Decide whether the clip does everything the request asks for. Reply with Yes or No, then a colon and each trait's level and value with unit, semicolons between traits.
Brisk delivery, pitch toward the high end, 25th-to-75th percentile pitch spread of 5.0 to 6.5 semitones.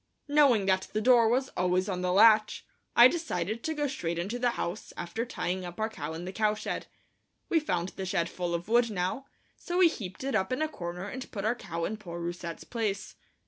Yes: fast, 220 wpm; high, 205 Hz; average, 5.3 semitones